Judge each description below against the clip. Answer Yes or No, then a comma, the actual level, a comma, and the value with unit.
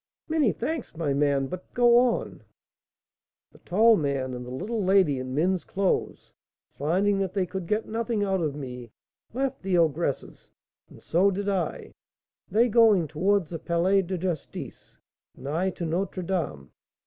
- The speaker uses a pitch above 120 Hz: Yes, medium, 185 Hz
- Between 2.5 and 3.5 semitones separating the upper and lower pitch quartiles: No, average, 4.9 semitones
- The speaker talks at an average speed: Yes, average, 160 wpm